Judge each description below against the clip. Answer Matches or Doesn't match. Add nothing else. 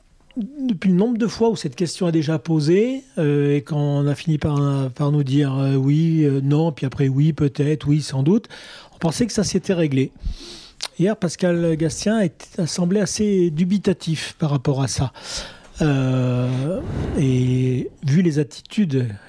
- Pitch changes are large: Doesn't match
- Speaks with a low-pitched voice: Doesn't match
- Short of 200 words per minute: Matches